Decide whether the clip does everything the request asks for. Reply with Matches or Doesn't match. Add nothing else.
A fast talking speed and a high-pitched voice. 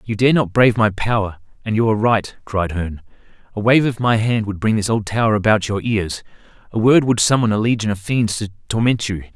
Doesn't match